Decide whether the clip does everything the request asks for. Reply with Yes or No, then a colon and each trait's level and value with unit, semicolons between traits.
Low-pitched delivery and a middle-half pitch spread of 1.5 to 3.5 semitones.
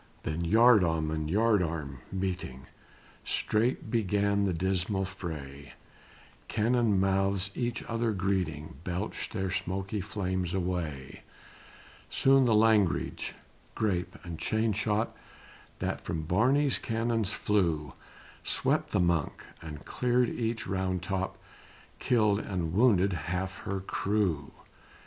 No: very low, 95 Hz; average, 3.9 semitones